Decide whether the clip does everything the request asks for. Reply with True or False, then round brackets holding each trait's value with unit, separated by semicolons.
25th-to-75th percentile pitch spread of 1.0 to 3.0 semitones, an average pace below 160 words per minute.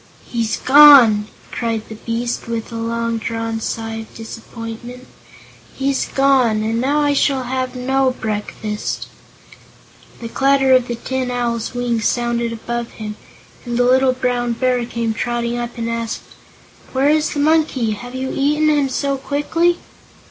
True (2.6 semitones; 150 wpm)